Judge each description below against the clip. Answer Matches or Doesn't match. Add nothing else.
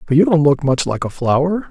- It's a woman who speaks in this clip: Doesn't match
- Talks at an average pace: Doesn't match